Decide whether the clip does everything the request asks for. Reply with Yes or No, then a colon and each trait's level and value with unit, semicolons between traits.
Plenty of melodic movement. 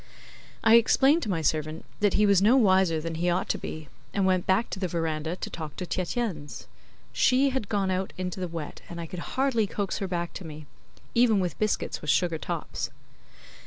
No: average, 4.1 semitones